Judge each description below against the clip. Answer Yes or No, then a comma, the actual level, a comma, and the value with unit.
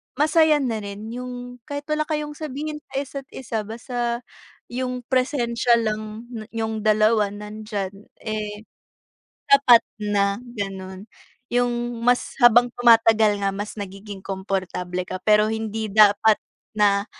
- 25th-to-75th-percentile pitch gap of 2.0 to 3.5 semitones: Yes, average, 3.1 semitones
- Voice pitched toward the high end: Yes, high, 220 Hz